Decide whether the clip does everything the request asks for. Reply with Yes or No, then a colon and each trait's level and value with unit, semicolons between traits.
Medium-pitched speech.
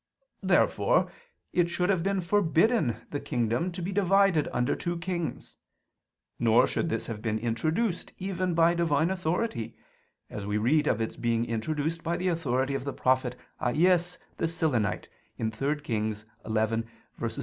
Yes: medium, 155 Hz